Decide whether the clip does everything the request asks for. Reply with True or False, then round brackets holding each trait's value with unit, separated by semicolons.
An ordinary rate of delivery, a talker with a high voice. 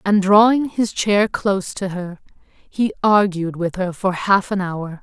True (180 wpm; 195 Hz)